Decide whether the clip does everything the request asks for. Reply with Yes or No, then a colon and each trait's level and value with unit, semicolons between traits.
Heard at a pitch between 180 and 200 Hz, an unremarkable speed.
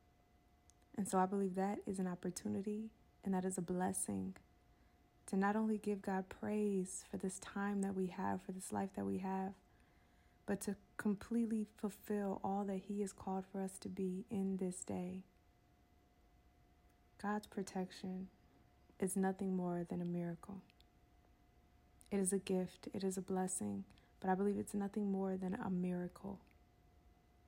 Yes: high, 190 Hz; average, 155 wpm